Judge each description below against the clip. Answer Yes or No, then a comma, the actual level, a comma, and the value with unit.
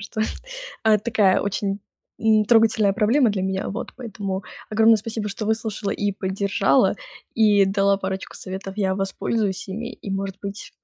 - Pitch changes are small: Yes, narrow, 2.1 semitones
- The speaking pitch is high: Yes, high, 205 Hz